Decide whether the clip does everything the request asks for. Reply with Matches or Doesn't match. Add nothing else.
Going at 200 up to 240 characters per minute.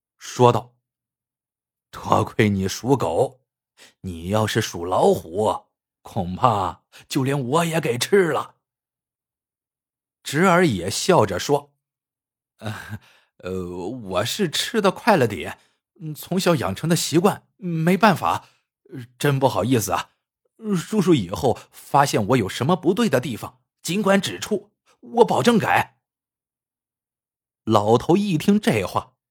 Doesn't match